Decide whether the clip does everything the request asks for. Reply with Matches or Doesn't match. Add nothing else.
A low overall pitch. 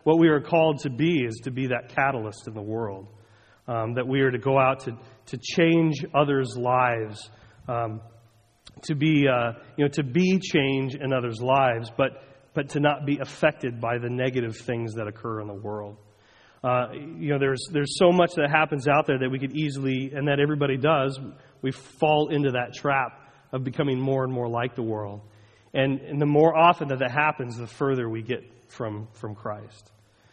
Matches